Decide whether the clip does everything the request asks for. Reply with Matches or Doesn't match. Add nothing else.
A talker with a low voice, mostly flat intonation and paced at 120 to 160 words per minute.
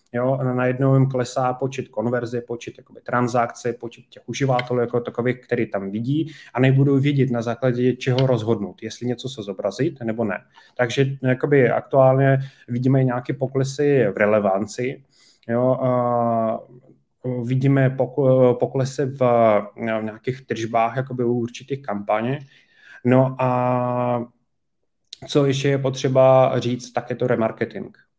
Matches